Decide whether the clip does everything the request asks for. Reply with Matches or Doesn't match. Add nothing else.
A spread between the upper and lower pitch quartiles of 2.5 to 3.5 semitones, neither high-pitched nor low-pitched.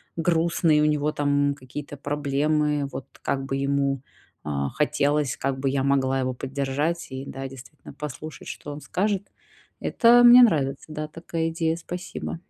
Matches